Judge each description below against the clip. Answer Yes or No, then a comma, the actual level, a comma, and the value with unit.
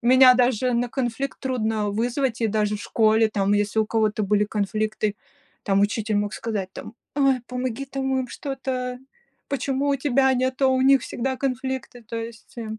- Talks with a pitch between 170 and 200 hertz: No, high, 240 Hz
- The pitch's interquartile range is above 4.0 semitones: No, average, 3.4 semitones